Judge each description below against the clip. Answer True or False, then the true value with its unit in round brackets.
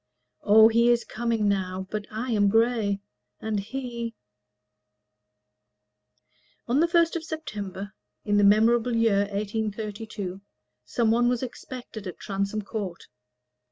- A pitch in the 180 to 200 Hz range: False (220 Hz)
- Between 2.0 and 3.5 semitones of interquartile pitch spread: True (2.8 semitones)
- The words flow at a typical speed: False (125 wpm)